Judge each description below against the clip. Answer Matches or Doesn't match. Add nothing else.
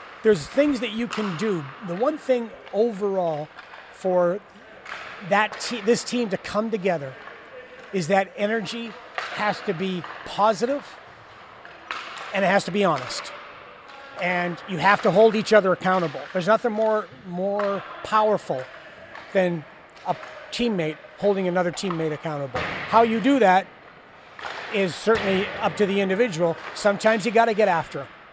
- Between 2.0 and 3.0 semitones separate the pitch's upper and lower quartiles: Doesn't match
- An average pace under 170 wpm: Matches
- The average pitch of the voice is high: Matches